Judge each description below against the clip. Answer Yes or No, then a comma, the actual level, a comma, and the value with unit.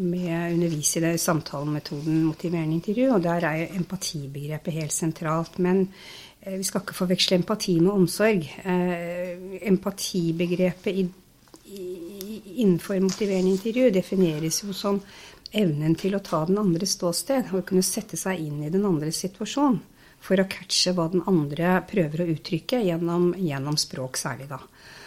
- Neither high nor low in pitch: Yes, medium, 180 Hz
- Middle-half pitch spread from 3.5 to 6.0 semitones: No, average, 2.7 semitones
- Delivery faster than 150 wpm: No, slow, 135 wpm